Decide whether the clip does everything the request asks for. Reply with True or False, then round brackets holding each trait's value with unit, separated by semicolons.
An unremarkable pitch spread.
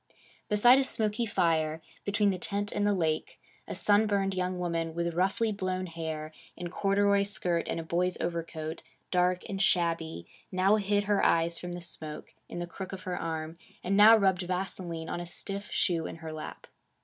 True (3.2 semitones)